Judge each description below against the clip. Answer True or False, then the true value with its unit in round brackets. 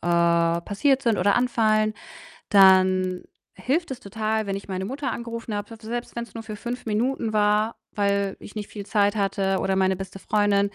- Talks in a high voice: True (205 Hz)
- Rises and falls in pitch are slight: False (3.0 semitones)